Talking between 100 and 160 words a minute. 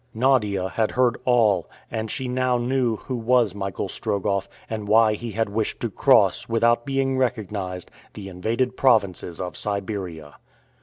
Yes: average, 150 wpm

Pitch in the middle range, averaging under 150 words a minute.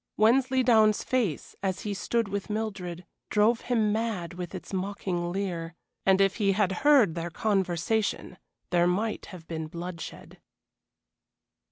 No: high, 195 Hz; slow, 135 wpm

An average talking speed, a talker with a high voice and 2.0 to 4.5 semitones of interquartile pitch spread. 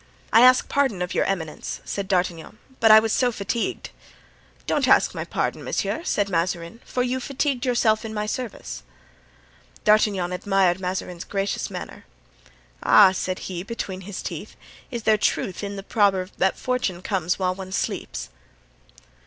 Yes: average, 155 wpm; high, 200 Hz; average, 3.5 semitones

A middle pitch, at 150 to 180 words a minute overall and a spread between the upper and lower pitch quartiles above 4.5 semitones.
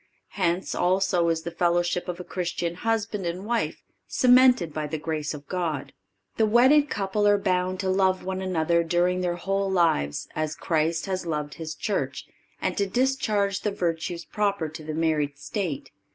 No: medium, 180 Hz; average, 170 wpm; average, 3.4 semitones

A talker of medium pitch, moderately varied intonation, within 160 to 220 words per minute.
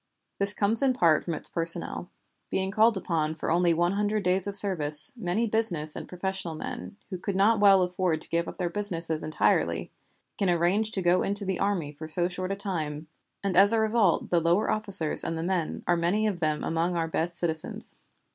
Yes: medium, 180 Hz; average, 3.3 semitones; fast, 205 wpm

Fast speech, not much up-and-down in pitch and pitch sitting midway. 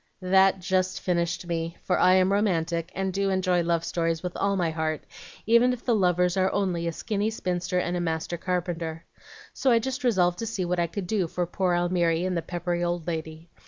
Yes: fast, 210 wpm; narrow, 2.2 semitones; medium, 180 Hz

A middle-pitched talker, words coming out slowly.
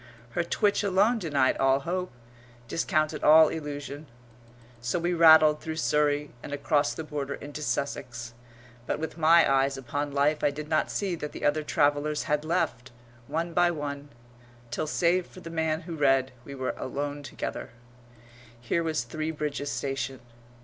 No: medium, 150 Hz; average, 160 wpm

